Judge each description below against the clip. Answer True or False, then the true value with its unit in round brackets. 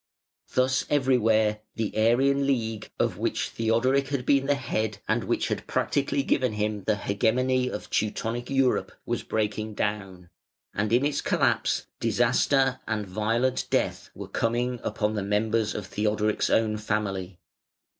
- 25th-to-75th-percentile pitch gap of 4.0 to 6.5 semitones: False (3.4 semitones)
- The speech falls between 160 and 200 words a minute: False (145 wpm)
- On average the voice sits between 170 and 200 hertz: False (110 Hz)